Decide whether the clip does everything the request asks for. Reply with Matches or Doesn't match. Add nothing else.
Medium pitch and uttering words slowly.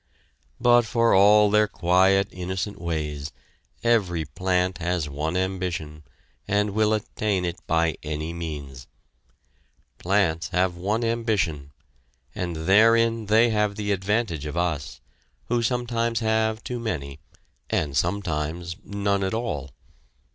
Doesn't match